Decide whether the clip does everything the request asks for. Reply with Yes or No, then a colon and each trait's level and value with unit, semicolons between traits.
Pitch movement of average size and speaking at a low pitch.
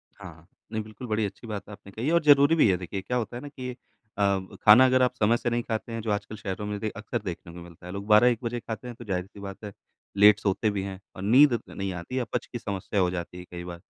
Yes: average, 3.8 semitones; low, 105 Hz